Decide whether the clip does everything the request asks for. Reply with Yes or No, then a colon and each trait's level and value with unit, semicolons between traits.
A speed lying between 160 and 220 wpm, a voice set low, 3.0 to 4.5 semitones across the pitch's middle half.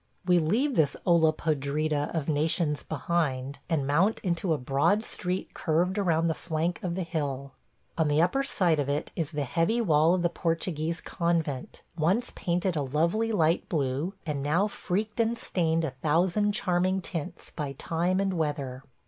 No: average, 170 wpm; medium, 165 Hz; average, 3.5 semitones